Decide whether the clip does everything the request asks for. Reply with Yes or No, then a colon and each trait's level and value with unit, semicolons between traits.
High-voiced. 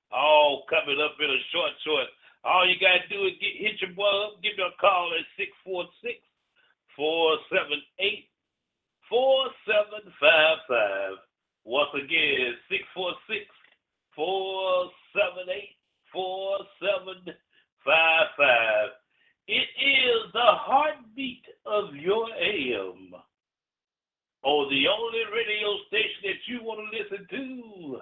Yes: high, 205 Hz